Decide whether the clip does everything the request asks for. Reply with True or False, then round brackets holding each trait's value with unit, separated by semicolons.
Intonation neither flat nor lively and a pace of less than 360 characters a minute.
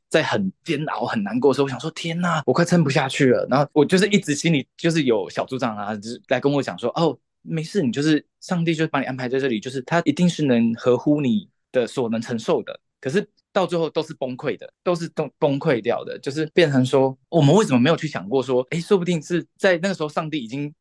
False (4.4 semitones; 370 characters per minute)